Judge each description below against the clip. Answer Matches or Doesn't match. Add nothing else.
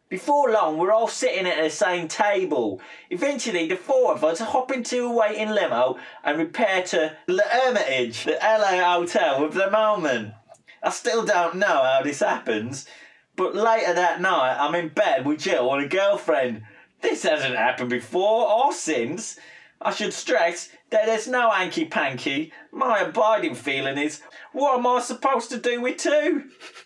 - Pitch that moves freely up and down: Matches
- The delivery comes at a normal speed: Matches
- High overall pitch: Matches